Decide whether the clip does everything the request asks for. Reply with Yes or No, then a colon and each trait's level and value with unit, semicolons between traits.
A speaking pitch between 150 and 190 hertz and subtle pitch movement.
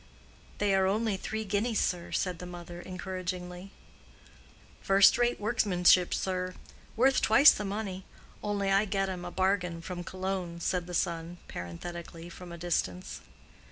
Yes: medium, 185 Hz; narrow, 2.1 semitones